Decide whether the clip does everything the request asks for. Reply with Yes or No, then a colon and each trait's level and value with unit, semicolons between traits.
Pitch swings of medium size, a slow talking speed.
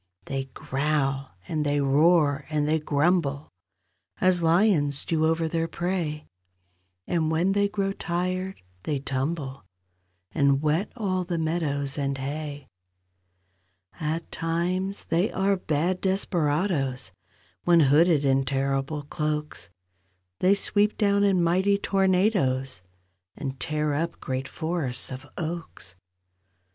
Yes: average, 4.3 semitones; slow, 115 wpm